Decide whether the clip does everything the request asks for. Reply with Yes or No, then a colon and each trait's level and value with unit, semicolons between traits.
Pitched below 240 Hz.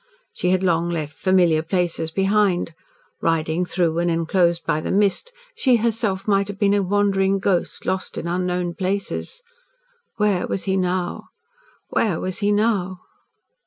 Yes: medium, 185 Hz